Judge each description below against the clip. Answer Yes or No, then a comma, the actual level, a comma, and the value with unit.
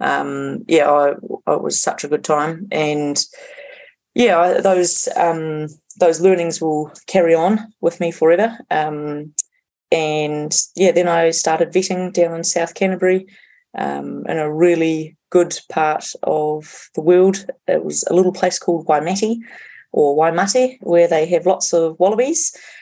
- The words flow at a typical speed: Yes, average, 145 wpm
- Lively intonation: No, average, 3.3 semitones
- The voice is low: No, medium, 170 Hz